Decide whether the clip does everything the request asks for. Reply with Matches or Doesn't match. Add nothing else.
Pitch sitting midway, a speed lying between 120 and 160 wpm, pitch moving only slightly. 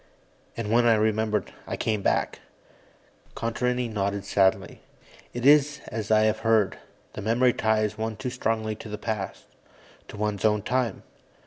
Doesn't match